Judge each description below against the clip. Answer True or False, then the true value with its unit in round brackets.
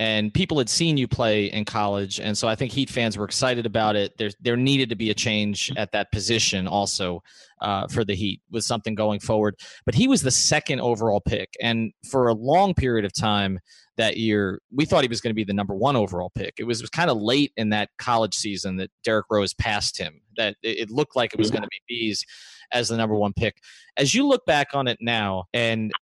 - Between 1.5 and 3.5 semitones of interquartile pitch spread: True (2.9 semitones)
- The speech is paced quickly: True (240 wpm)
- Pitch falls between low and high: False (110 Hz)